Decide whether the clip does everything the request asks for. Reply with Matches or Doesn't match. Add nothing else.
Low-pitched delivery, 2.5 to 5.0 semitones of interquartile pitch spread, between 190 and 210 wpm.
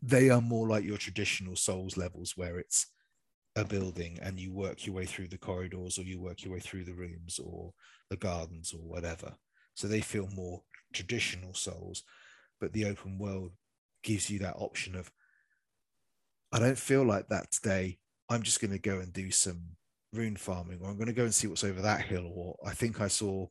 Matches